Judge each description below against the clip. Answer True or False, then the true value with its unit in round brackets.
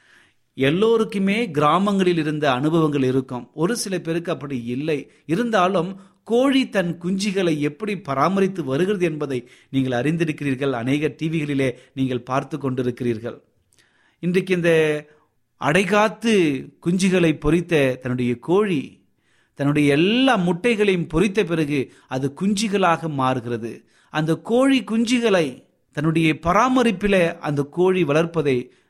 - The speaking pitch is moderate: True (160 Hz)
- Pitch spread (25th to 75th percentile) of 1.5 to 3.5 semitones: False (5.6 semitones)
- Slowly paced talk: False (100 wpm)